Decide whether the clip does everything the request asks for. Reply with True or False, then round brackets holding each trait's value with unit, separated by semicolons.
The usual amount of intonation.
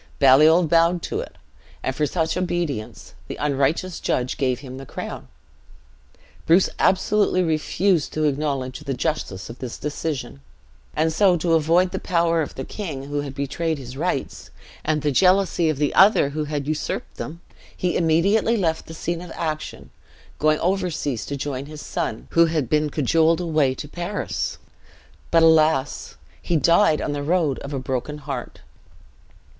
True (3.3 semitones)